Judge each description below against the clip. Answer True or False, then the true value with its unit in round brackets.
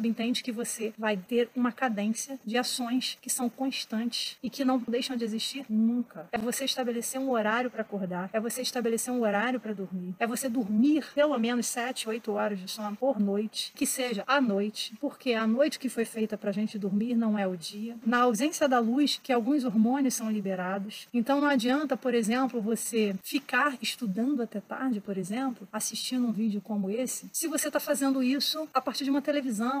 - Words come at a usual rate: False (195 wpm)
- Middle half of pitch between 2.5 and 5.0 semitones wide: True (3.3 semitones)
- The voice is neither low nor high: False (240 Hz)